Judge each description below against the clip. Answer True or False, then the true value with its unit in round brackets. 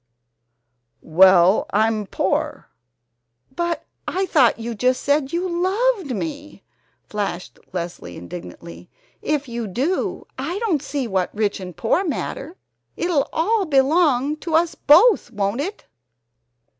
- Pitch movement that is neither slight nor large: False (8.7 semitones)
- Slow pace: True (120 wpm)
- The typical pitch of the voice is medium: False (275 Hz)